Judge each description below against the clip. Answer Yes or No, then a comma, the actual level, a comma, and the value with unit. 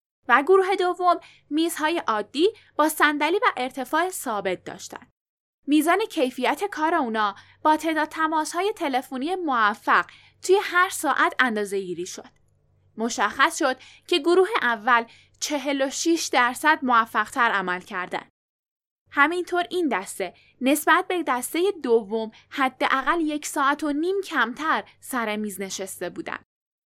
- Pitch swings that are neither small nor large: No, wide, 6.2 semitones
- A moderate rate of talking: Yes, average, 125 wpm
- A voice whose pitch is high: Yes, very high, 285 Hz